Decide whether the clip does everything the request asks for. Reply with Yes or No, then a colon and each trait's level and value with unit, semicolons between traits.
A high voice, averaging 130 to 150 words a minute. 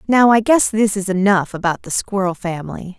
No: high, 200 Hz; average, 200 wpm